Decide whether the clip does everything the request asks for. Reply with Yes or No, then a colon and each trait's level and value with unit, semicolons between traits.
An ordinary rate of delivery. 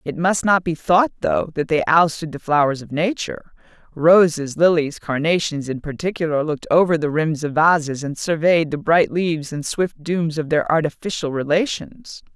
Yes: average, 175 wpm